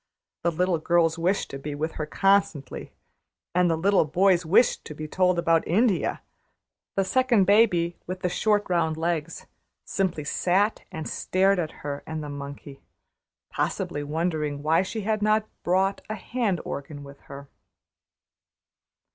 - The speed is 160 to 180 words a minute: No, average, 145 wpm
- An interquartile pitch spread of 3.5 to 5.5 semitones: Yes, average, 4.1 semitones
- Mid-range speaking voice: Yes, medium, 170 Hz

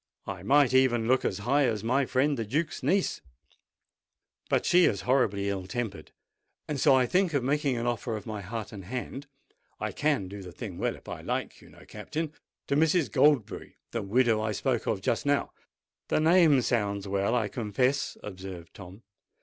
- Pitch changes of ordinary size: No, wide, 5.7 semitones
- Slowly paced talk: No, average, 180 wpm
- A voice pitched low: Yes, low, 120 Hz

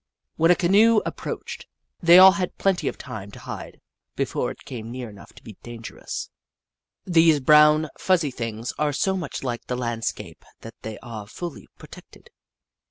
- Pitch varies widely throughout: Yes, wide, 7.0 semitones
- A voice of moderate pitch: Yes, medium, 145 Hz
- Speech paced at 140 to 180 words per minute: Yes, average, 165 wpm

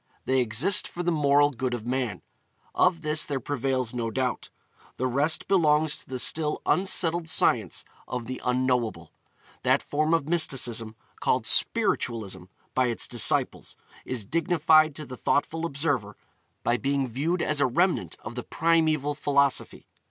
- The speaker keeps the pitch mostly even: No, average, 4.2 semitones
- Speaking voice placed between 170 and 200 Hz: No, medium, 140 Hz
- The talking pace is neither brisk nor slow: Yes, average, 150 wpm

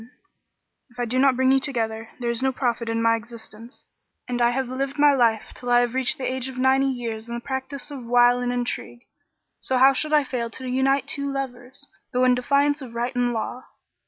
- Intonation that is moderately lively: No, narrow, 2.0 semitones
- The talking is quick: Yes, fast, 225 wpm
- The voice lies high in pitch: Yes, very high, 250 Hz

